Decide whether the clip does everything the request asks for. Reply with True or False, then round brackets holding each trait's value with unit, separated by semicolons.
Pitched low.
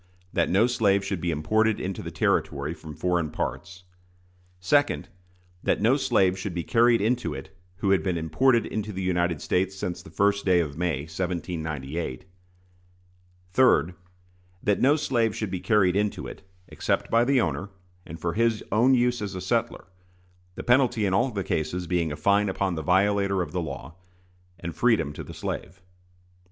True (95 Hz)